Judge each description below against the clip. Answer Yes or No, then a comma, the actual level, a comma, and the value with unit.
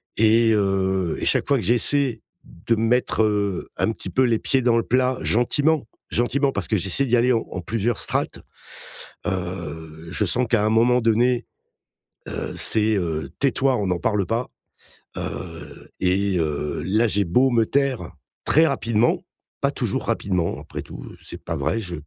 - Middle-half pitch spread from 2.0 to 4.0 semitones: No, average, 4.6 semitones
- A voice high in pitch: No, low, 110 Hz